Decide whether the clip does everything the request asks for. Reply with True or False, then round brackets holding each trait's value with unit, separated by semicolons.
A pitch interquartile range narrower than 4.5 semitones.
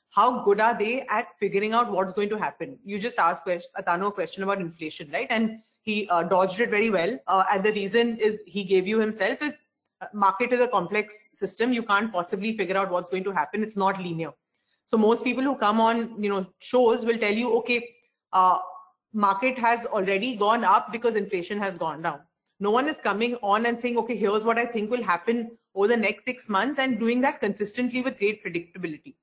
True (3.3 semitones)